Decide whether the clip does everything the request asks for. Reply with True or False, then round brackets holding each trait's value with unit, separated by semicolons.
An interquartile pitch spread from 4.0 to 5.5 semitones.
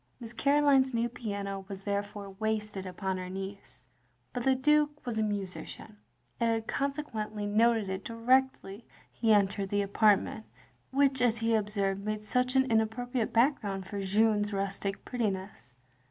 False (3.5 semitones)